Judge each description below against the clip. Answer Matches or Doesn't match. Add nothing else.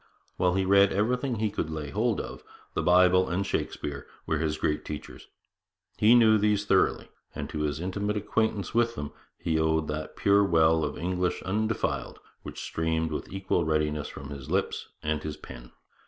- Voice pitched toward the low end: Matches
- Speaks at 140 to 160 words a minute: Doesn't match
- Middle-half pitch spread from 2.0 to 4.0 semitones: Doesn't match